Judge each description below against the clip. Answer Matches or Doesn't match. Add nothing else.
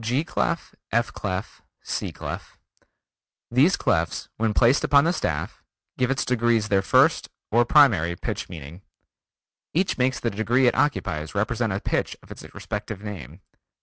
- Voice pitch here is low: Matches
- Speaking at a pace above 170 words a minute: Doesn't match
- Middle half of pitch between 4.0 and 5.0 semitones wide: Matches